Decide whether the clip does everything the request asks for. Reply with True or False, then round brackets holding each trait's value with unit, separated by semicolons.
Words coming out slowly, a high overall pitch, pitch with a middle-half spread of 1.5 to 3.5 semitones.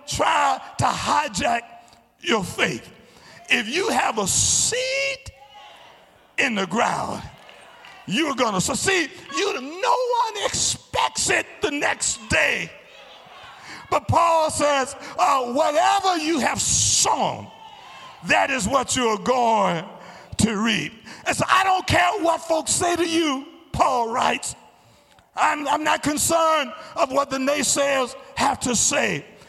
False (130 wpm; 305 Hz; 4.4 semitones)